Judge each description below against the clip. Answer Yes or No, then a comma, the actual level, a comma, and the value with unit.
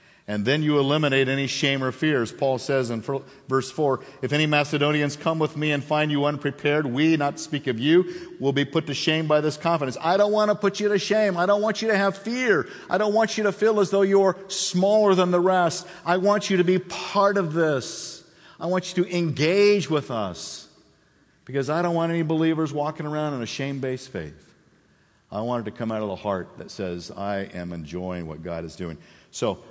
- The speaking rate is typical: No, fast, 225 wpm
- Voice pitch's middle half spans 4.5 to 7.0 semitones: Yes, wide, 5.4 semitones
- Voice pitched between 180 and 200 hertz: No, medium, 150 Hz